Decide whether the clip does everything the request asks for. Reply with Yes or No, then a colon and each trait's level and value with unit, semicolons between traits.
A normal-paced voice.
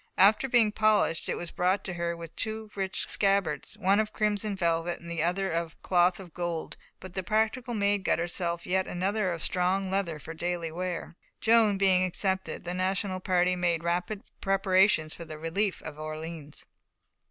Yes: average, 175 wpm